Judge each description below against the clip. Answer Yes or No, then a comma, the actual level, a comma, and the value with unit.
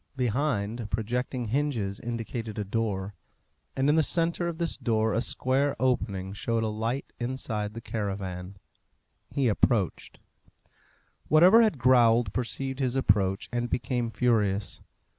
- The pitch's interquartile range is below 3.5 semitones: No, average, 3.9 semitones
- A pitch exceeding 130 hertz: No, low, 115 Hz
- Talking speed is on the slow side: Yes, slow, 130 wpm